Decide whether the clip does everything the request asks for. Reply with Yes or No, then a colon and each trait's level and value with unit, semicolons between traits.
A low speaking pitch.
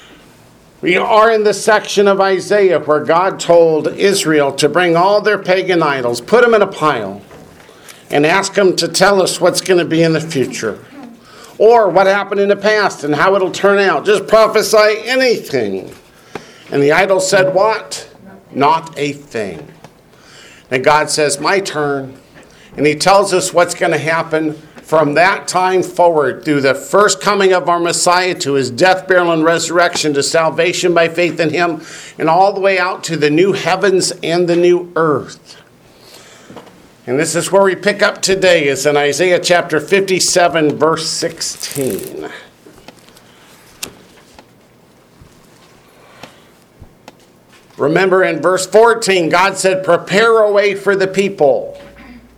No: medium, 180 Hz